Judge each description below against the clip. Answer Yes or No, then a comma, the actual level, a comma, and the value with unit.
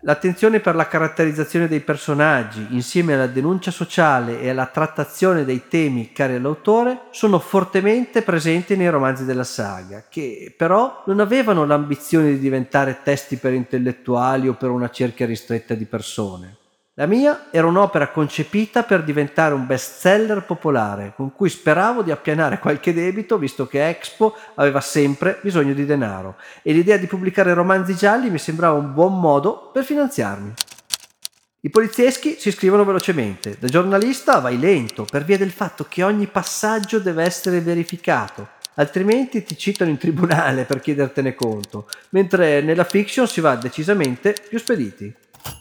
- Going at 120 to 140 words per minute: No, average, 150 wpm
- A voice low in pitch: No, medium, 160 Hz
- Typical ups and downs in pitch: No, wide, 6.6 semitones